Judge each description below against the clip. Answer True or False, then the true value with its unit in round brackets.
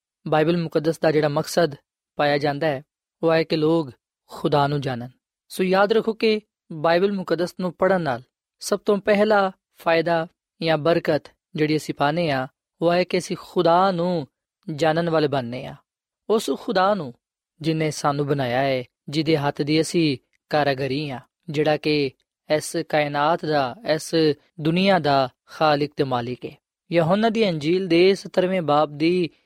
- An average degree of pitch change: True (3.4 semitones)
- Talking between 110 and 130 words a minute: True (115 wpm)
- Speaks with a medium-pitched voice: True (160 Hz)